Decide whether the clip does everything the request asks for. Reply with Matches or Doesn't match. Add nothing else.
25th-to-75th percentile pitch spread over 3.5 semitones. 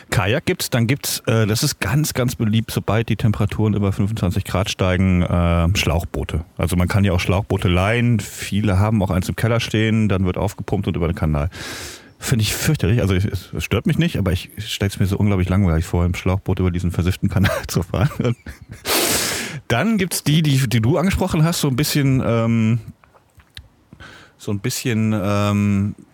Matches